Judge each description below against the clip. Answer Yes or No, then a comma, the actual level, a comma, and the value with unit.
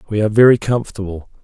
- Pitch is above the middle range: No, low, 105 Hz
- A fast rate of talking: No, average, 170 wpm